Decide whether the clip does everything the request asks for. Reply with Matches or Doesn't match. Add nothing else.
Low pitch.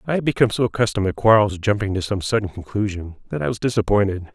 Matches